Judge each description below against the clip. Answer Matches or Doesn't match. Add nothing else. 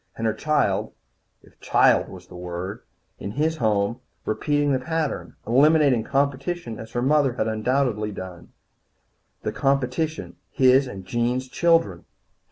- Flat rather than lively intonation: Doesn't match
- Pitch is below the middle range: Matches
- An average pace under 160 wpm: Matches